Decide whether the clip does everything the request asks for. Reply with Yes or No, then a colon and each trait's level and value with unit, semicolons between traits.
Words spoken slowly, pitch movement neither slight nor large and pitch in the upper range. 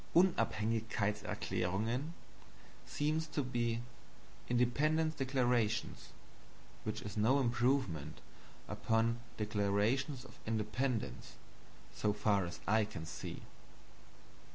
No: slow, 80 wpm; average, 3.8 semitones; low, 115 Hz